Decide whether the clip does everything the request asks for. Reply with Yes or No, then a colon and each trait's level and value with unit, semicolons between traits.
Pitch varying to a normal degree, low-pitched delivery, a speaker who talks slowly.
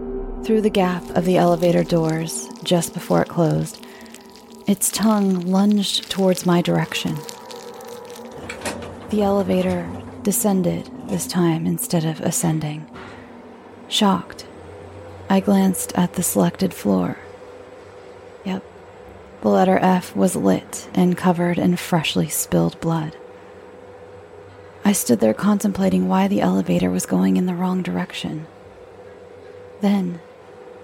No: average, 4.2 semitones; medium, 185 Hz; slow, 115 wpm